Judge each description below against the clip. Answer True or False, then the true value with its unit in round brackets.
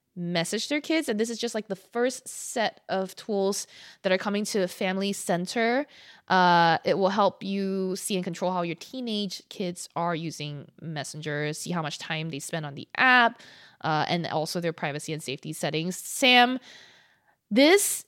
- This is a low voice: False (185 Hz)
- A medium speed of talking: True (180 wpm)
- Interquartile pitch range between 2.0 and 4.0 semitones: False (4.8 semitones)